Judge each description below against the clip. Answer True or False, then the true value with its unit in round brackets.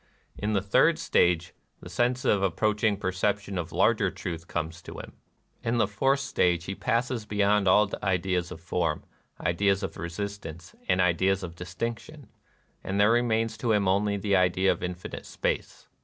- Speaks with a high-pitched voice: False (95 Hz)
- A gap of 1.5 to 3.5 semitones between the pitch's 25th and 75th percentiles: True (3.0 semitones)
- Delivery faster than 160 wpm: True (170 wpm)